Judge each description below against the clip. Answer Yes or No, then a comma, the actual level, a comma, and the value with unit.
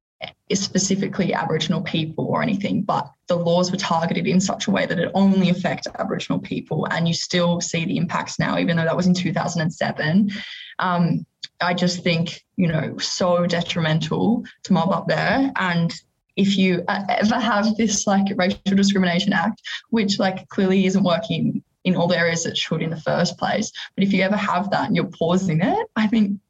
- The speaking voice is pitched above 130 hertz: Yes, medium, 185 Hz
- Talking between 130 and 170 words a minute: No, average, 190 wpm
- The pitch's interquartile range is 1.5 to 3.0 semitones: Yes, narrow, 2.6 semitones